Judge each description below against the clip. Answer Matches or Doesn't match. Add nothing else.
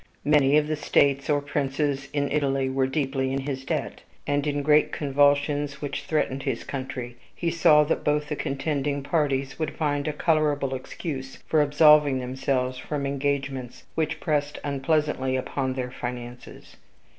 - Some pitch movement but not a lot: Doesn't match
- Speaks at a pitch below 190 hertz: Matches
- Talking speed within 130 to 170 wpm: Matches